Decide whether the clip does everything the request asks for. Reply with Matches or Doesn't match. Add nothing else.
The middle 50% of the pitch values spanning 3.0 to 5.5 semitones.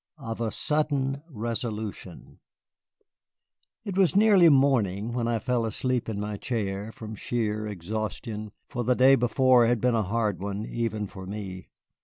Matches